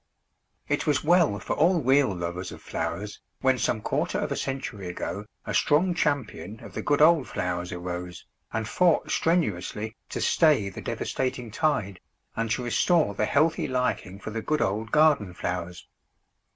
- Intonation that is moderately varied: No, wide, 7.7 semitones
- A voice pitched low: Yes, low, 115 Hz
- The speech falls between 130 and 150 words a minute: No, average, 165 wpm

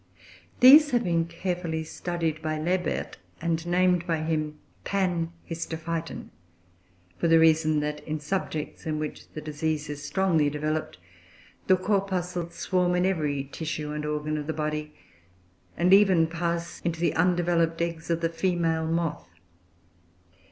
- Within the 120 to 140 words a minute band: Yes, slow, 135 wpm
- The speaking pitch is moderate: Yes, medium, 165 Hz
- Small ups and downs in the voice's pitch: Yes, narrow, 2.3 semitones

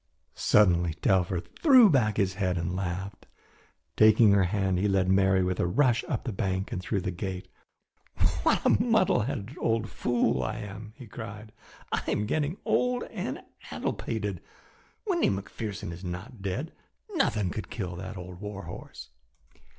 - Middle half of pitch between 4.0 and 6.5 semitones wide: No, average, 3.6 semitones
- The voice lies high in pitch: No, low, 100 Hz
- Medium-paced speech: Yes, average, 160 wpm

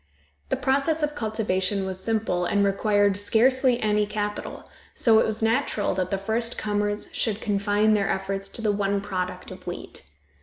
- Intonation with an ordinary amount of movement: No, narrow, 2.1 semitones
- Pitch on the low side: No, high, 210 Hz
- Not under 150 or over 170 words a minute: Yes, average, 165 wpm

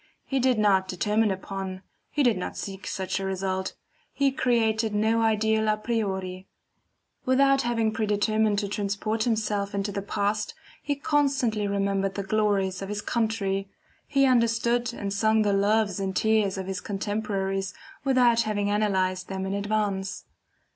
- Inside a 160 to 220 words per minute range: No, average, 150 wpm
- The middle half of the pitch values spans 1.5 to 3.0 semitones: Yes, narrow, 2.4 semitones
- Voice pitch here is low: No, high, 210 Hz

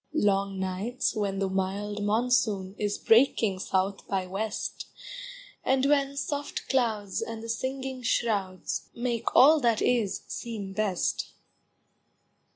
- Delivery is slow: Yes, slow, 120 wpm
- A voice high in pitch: Yes, high, 215 Hz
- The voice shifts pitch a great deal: No, average, 4.1 semitones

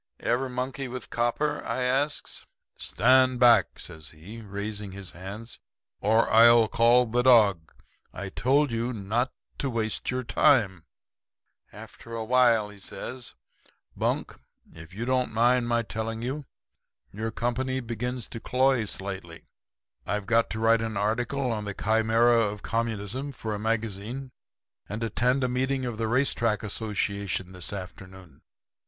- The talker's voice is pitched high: No, low, 115 Hz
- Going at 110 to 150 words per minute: Yes, average, 145 wpm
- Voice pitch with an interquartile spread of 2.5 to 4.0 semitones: Yes, average, 3.3 semitones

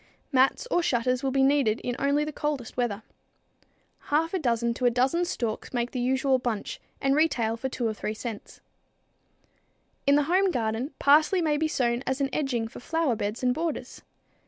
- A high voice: Yes, very high, 260 Hz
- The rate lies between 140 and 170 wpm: No, average, 185 wpm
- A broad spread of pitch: No, average, 3.8 semitones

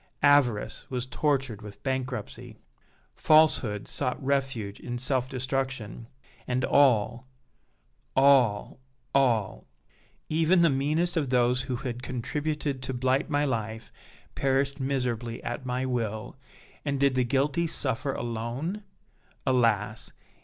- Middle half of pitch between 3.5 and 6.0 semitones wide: No, average, 2.7 semitones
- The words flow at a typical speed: No, slow, 115 wpm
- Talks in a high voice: No, low, 130 Hz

